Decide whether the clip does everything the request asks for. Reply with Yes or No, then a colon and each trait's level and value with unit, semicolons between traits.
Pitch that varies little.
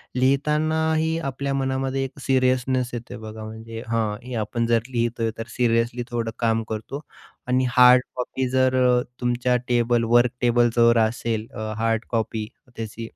Yes: narrow, 2.2 semitones